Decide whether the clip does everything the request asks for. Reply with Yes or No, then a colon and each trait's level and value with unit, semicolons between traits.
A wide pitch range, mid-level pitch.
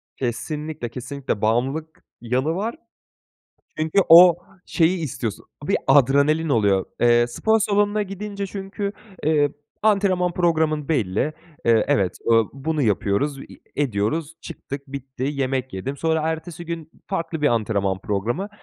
Yes: wide, 5.8 semitones; medium, 145 Hz